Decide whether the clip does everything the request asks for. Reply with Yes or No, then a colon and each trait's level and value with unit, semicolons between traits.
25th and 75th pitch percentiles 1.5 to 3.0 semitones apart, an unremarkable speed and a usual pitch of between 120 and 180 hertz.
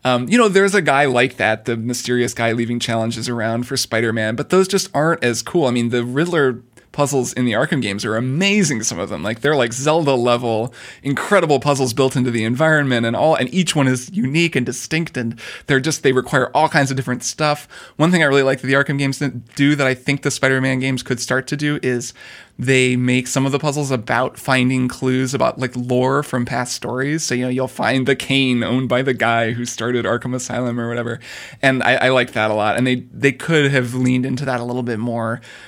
No: narrow, 2.5 semitones; fast, 235 wpm; low, 130 Hz